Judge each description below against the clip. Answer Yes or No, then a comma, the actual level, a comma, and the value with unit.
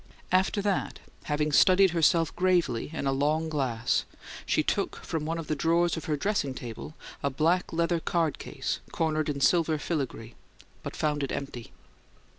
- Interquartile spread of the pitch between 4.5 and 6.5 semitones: No, average, 3.2 semitones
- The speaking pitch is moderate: Yes, medium, 155 Hz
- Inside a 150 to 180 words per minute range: Yes, average, 165 wpm